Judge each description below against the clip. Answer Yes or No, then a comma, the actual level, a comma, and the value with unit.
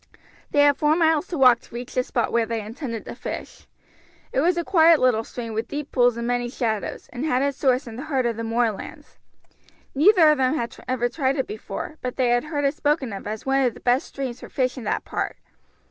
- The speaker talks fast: Yes, fast, 240 wpm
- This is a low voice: No, very high, 255 Hz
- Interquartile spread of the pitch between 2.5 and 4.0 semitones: Yes, average, 3.5 semitones